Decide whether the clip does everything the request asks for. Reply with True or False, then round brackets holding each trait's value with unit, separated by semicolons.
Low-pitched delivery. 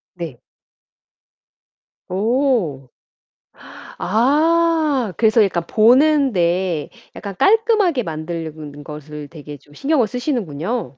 False (205 Hz)